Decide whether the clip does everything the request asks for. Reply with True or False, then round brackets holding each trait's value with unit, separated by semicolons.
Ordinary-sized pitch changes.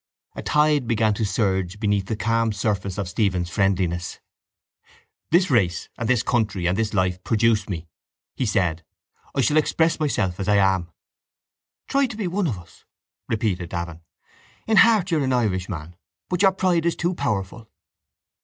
False (7.4 semitones)